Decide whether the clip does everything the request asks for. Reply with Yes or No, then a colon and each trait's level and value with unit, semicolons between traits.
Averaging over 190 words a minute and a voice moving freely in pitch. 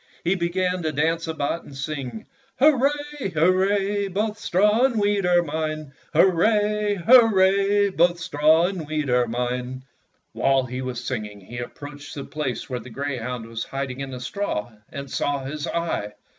No: average, 165 wpm; wide, 6.8 semitones